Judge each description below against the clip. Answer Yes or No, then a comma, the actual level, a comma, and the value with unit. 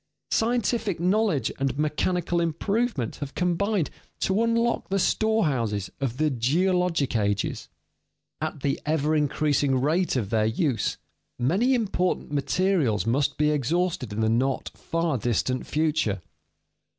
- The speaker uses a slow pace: Yes, slow, 125 wpm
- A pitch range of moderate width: No, wide, 6.2 semitones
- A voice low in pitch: No, medium, 155 Hz